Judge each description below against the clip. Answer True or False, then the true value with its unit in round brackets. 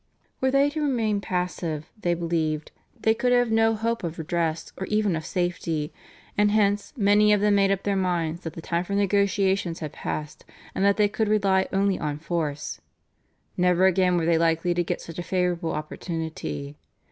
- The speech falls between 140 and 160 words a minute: False (185 wpm)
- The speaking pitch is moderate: True (180 Hz)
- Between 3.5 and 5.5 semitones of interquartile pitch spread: True (3.8 semitones)